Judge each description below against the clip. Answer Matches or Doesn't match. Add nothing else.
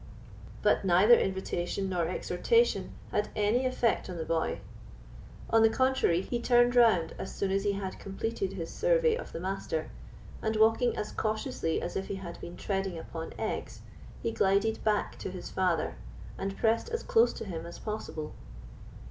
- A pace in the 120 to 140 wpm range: Doesn't match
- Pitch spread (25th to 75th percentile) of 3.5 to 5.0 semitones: Matches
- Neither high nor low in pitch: Doesn't match